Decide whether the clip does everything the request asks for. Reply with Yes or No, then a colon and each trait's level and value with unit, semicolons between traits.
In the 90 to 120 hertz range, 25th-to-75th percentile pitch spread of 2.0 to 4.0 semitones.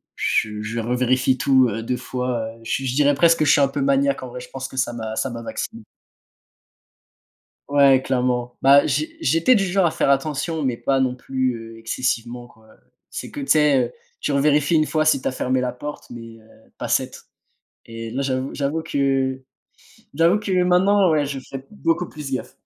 No: low, 135 Hz; average, 3.3 semitones